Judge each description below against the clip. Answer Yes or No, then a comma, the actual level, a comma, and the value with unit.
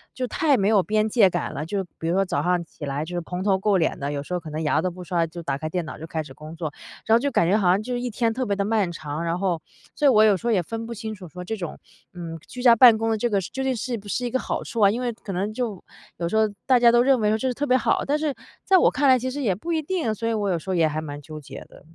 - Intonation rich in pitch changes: Yes, wide, 5.8 semitones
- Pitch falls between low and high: No, high, 205 Hz